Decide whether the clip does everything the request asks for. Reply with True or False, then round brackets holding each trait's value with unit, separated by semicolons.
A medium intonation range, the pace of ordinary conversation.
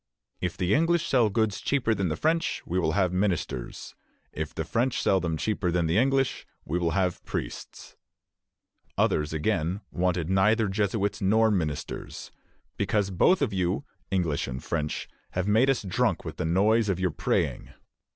True (4.2 semitones; 165 wpm)